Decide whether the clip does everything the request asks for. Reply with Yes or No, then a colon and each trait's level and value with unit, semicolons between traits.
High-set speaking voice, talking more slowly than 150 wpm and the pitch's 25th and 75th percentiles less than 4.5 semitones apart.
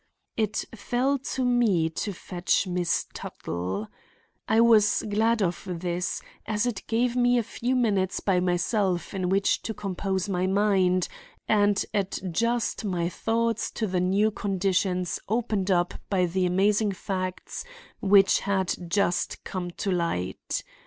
Yes: high, 195 Hz; average, 140 wpm; average, 3.2 semitones